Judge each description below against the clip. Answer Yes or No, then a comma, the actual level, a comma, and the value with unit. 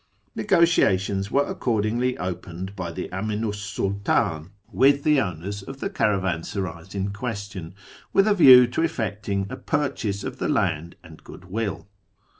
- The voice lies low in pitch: Yes, low, 100 Hz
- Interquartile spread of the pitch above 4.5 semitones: Yes, average, 5.0 semitones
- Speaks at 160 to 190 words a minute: No, average, 140 wpm